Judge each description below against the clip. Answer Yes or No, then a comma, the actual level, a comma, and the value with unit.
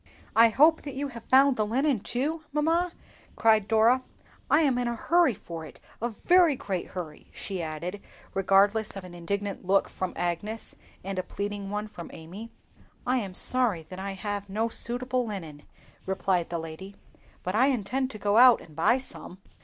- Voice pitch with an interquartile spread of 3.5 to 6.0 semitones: Yes, average, 5.1 semitones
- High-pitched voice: Yes, high, 210 Hz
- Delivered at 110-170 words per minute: No, average, 180 wpm